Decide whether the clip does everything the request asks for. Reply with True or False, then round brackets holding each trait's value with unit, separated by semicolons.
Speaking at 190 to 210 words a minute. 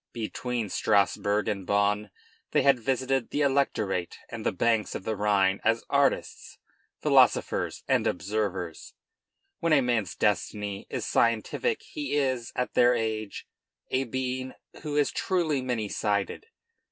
False (135 wpm)